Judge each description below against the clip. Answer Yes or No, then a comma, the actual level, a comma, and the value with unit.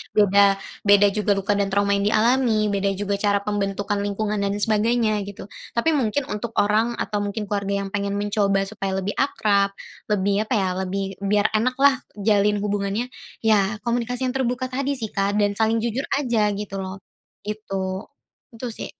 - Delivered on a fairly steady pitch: Yes, narrow, 2.2 semitones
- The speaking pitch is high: Yes, high, 210 Hz